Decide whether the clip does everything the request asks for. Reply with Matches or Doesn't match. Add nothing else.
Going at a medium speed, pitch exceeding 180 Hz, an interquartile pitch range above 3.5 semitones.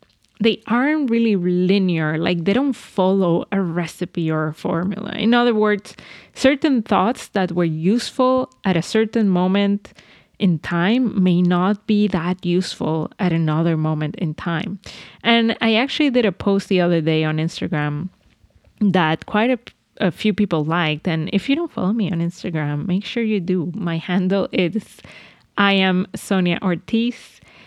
Matches